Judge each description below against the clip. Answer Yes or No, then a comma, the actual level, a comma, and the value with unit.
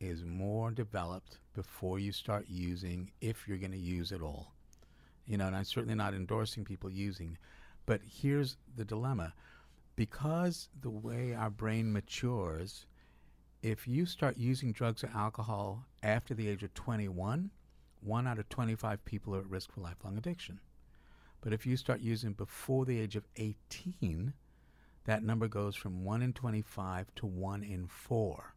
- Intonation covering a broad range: No, average, 3.8 semitones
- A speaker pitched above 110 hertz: No, low, 105 Hz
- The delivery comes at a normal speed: Yes, average, 160 wpm